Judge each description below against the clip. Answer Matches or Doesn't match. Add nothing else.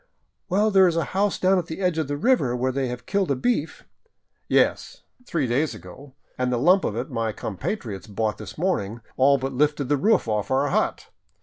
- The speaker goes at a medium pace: Doesn't match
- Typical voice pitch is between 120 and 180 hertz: Matches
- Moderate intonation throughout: Doesn't match